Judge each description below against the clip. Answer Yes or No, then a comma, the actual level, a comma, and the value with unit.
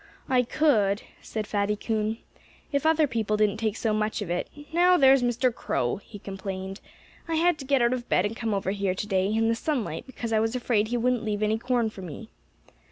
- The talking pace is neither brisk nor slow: No, fast, 220 wpm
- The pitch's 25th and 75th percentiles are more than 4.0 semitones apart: No, average, 3.4 semitones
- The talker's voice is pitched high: Yes, high, 220 Hz